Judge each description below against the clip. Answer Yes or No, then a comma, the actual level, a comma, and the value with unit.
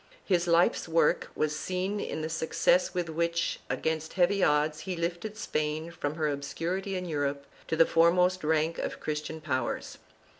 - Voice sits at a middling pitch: Yes, medium, 165 Hz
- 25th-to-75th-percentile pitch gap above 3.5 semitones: No, average, 2.7 semitones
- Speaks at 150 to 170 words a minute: Yes, average, 160 wpm